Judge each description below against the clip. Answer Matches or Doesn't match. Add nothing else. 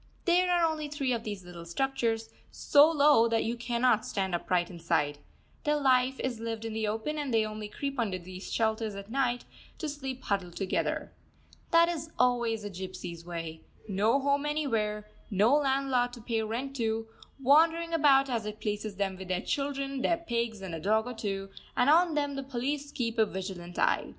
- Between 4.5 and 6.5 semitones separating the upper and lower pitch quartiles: Matches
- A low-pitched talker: Doesn't match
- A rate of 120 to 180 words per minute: Doesn't match